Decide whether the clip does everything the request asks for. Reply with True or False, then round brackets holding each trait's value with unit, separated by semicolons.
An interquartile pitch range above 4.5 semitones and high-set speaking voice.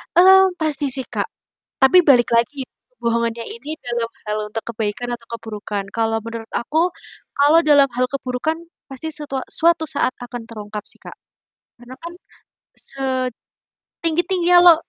True (5.5 semitones; 260 Hz)